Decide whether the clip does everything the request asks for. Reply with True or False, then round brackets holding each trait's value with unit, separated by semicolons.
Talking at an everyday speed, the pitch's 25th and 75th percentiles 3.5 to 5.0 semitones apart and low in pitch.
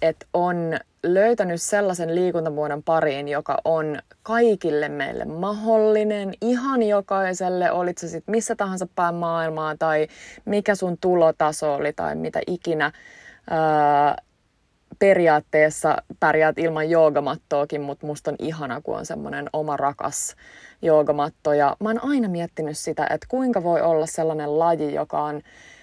False (130 wpm; 4.0 semitones; 165 Hz)